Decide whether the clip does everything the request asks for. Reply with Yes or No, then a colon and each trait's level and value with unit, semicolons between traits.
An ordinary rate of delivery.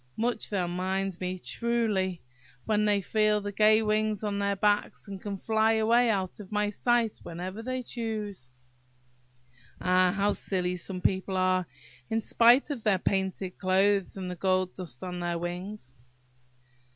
Yes: average, 155 wpm